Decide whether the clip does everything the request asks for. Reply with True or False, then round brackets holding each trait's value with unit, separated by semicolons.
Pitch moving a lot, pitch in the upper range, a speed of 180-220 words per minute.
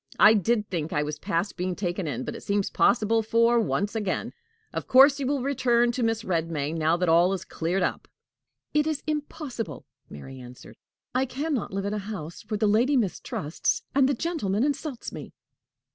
True (6.7 semitones; 210 Hz; 190 wpm)